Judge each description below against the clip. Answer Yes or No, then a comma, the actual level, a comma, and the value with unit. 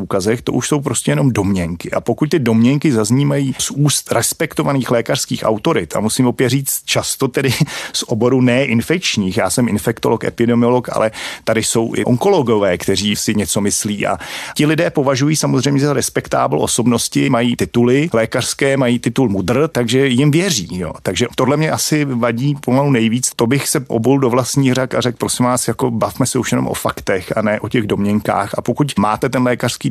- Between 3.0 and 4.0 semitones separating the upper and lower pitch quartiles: Yes, average, 3.7 semitones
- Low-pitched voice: Yes, low, 125 Hz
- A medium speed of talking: No, fast, 185 wpm